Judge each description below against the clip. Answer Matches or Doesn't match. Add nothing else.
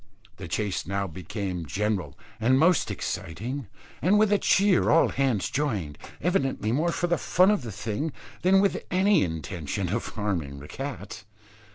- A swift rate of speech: Doesn't match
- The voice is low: Matches